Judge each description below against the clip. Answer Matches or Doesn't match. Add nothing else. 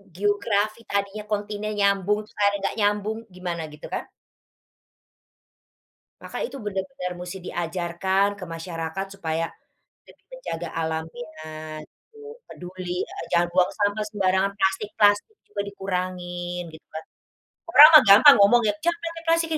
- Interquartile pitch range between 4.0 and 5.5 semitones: Doesn't match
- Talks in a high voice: Matches